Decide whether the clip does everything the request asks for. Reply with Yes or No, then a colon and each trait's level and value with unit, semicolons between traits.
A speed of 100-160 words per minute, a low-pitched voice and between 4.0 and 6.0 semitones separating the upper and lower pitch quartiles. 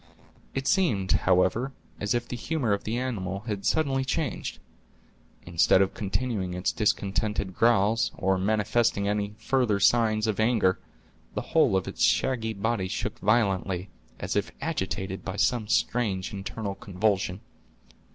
No: average, 140 wpm; low, 105 Hz; average, 3.6 semitones